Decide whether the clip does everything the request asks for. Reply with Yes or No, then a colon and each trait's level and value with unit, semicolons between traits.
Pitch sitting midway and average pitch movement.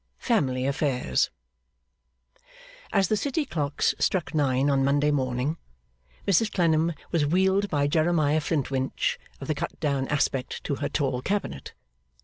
Yes: medium, 145 Hz; average, 4.1 semitones